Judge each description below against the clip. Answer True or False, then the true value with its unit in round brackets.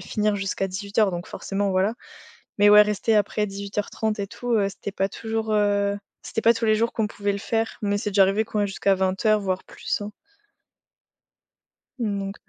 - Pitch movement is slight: True (1.6 semitones)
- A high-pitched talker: True (205 Hz)